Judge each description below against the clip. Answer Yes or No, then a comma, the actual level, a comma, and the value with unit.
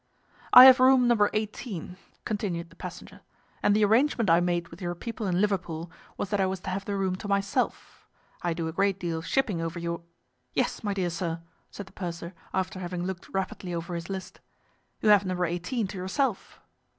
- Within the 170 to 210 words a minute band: Yes, average, 200 wpm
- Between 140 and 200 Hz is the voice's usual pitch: Yes, high, 190 Hz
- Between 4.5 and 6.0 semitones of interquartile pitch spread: No, average, 3.1 semitones